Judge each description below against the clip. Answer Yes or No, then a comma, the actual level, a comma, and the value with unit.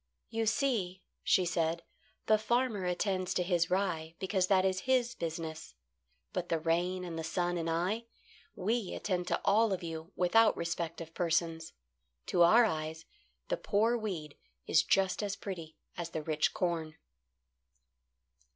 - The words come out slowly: No, average, 150 wpm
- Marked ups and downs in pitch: No, average, 3.6 semitones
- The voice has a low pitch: No, medium, 180 Hz